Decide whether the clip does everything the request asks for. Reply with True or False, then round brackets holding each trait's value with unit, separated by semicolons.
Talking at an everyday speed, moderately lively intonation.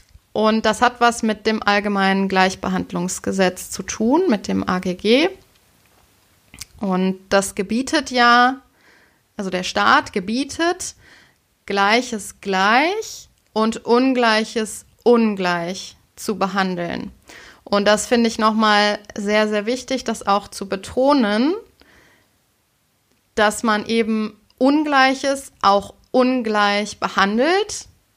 False (100 wpm; 3.9 semitones)